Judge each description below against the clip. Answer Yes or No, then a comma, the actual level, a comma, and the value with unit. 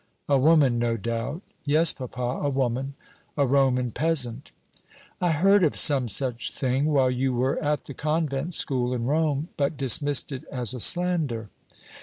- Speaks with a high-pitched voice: No, low, 135 Hz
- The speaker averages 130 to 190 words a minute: Yes, average, 160 wpm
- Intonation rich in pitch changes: No, average, 3.4 semitones